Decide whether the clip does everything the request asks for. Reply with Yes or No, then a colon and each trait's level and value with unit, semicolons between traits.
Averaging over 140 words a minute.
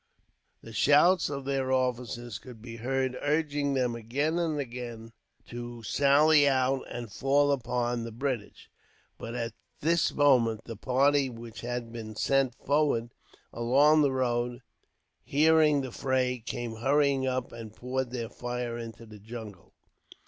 No: slow, 135 wpm